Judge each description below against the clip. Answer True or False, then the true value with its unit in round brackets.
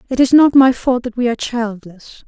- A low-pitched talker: False (240 Hz)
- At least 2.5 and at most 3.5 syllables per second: False (5.4 syllables/s)